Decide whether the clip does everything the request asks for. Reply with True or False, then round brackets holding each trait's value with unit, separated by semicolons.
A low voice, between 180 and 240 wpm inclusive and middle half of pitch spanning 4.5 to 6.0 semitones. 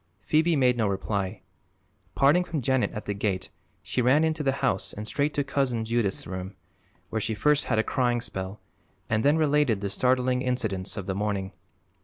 True (120 Hz; 185 wpm; 5.5 semitones)